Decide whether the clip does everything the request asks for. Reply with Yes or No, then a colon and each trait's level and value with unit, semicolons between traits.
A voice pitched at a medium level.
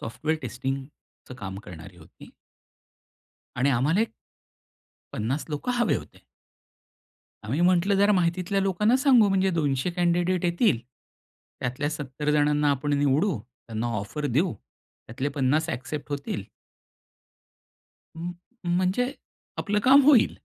Yes: medium, 150 Hz